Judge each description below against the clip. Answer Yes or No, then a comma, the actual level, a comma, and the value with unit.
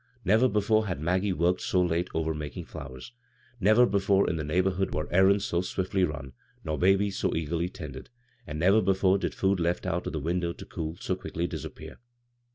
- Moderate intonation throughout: Yes, average, 3.2 semitones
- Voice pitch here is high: No, very low, 90 Hz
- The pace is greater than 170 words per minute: Yes, average, 195 wpm